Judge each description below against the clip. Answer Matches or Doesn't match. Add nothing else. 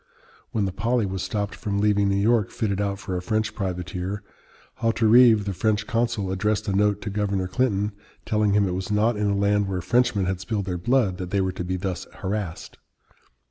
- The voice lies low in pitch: Matches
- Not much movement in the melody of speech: Matches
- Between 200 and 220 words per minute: Matches